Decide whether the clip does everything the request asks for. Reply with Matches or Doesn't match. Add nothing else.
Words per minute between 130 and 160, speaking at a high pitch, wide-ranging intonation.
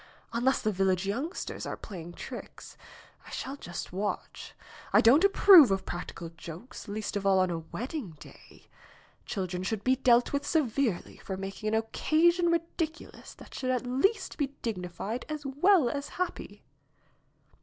Matches